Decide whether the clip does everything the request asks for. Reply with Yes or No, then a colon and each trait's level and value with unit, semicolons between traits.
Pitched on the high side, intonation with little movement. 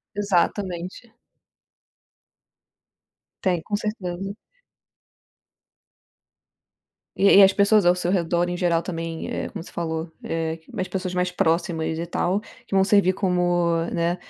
No: medium, 180 Hz; narrow, 2.3 semitones